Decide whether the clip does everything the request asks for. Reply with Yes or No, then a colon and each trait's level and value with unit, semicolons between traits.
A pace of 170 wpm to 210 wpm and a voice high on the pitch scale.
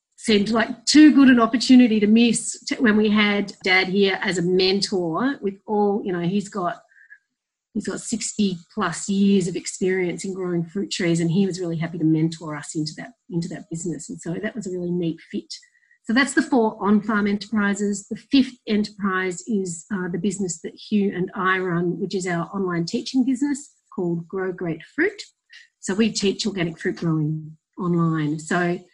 Yes: average, 190 wpm; high, 195 Hz